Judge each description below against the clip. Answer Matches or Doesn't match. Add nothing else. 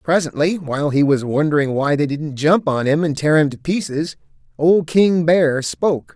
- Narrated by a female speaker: Doesn't match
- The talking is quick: Doesn't match